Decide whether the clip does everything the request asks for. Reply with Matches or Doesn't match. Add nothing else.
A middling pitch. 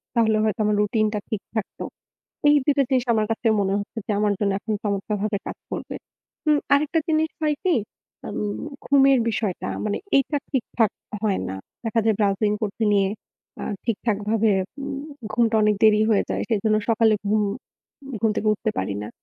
Doesn't match